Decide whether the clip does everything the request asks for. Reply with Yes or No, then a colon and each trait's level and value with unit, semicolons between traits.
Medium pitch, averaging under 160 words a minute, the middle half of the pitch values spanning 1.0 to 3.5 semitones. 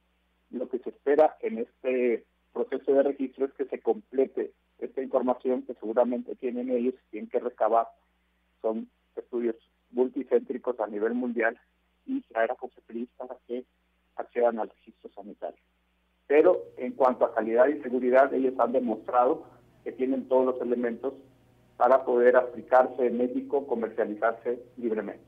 No: low, 125 Hz; average, 140 wpm; narrow, 2.5 semitones